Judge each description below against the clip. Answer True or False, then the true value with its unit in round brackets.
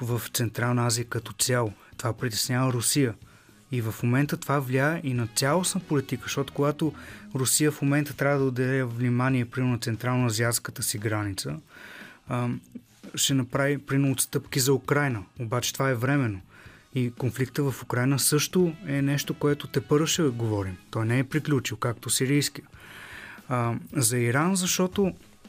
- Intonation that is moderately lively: True (3.2 semitones)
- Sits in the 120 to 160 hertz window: True (130 Hz)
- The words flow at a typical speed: True (145 wpm)